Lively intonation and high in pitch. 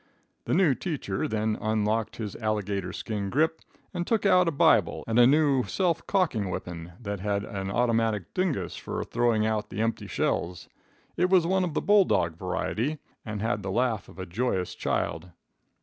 No: wide, 7.2 semitones; low, 110 Hz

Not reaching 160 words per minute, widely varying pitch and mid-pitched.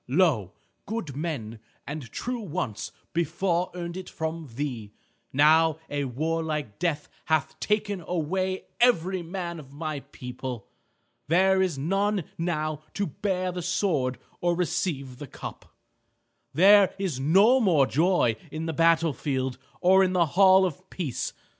No: average, 140 wpm; average, 4.5 semitones; medium, 165 Hz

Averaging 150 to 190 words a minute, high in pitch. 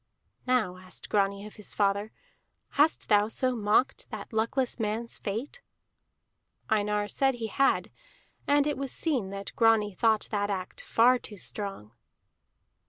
No: average, 140 wpm; high, 215 Hz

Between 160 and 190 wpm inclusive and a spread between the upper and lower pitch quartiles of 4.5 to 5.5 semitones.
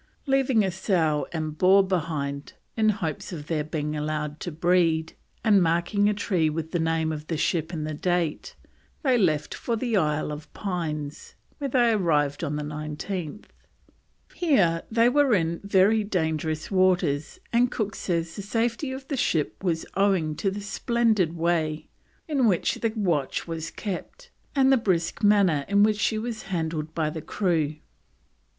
Yes: average, 165 wpm; average, 5.1 semitones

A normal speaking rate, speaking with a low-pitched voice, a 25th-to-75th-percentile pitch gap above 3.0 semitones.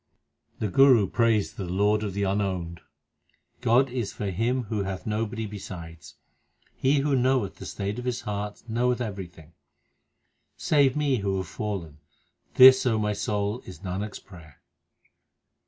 Yes: average, 155 wpm; low, 105 Hz; average, 4.1 semitones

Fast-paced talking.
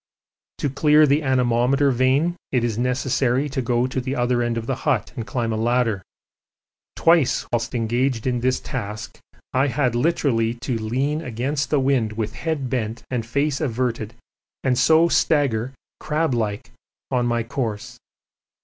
No: average, 160 wpm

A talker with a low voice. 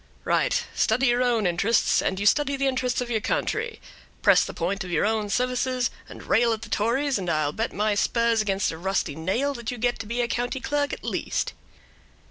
No: high, 230 Hz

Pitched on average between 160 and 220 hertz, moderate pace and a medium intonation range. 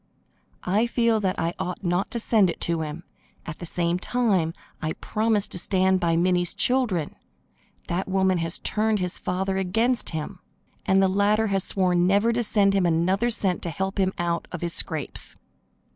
Yes: high, 190 Hz; average, 180 wpm; average, 3.1 semitones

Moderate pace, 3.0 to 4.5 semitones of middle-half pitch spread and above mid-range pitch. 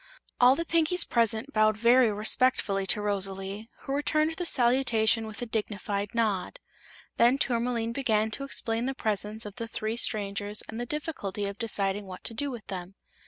Yes: average, 170 wpm; average, 3.4 semitones; high, 225 Hz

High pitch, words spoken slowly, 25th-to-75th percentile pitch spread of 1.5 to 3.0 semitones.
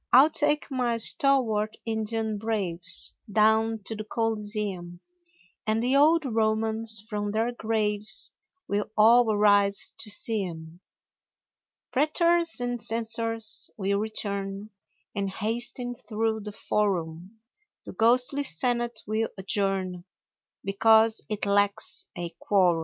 Yes: high, 220 Hz; slow, 115 wpm; narrow, 2.4 semitones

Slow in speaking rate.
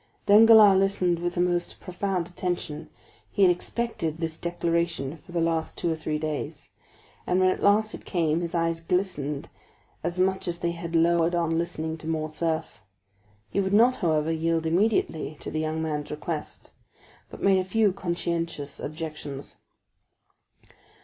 No: average, 155 wpm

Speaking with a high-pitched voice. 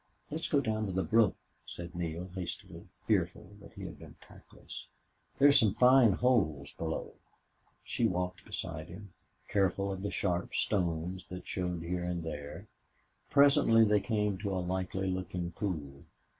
No: very low, 95 Hz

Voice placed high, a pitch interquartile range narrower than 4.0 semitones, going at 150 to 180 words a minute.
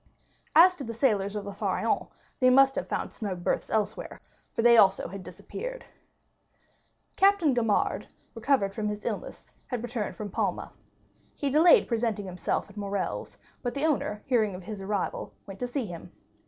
No: high, 225 Hz; average, 4.9 semitones; average, 170 wpm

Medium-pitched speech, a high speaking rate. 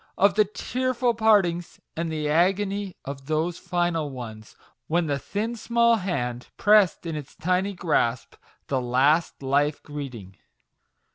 No: medium, 170 Hz; slow, 135 wpm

